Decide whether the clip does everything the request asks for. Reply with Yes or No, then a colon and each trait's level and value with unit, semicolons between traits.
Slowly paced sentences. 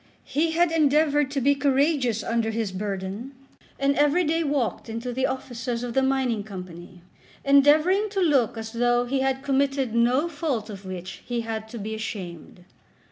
No: average, 170 wpm